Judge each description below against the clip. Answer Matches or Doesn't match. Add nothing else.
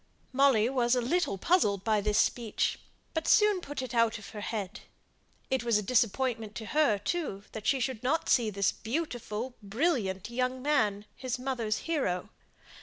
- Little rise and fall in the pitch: Doesn't match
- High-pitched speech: Matches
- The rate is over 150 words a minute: Matches